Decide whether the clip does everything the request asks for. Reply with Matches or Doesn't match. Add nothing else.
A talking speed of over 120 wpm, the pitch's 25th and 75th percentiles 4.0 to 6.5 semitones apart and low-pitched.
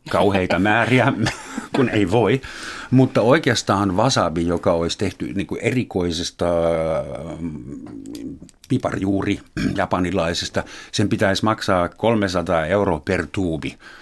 Doesn't match